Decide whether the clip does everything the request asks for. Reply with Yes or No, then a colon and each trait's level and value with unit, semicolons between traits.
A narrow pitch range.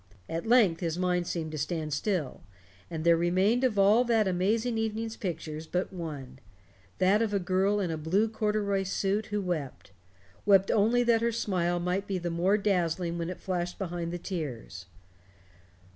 No: average, 3.7 semitones